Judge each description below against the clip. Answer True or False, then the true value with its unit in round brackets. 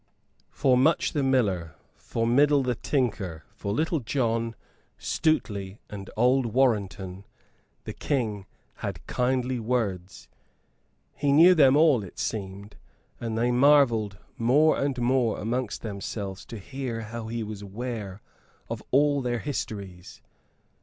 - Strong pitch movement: False (4.5 semitones)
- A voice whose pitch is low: True (115 Hz)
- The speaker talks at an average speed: False (125 wpm)